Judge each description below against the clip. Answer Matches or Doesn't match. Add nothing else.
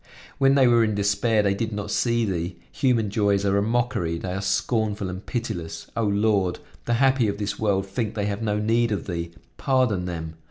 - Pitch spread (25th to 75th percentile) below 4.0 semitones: Matches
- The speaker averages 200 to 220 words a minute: Matches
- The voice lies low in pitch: Matches